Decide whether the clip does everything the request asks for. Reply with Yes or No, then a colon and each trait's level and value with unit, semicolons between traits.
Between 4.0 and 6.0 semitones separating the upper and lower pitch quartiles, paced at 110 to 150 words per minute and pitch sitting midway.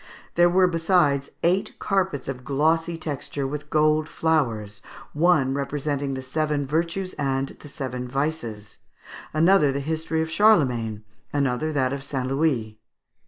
No: average, 3.2 semitones; slow, 135 wpm; medium, 145 Hz